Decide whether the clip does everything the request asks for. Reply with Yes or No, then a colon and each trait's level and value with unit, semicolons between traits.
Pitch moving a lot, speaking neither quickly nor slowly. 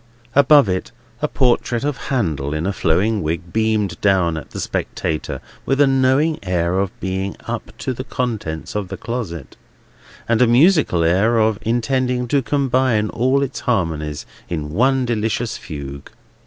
Yes: wide, 6.8 semitones; average, 155 wpm